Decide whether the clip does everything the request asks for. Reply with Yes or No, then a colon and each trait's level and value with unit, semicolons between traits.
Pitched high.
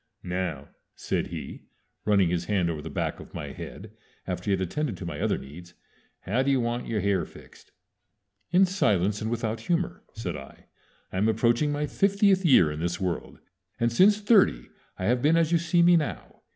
No: low, 110 Hz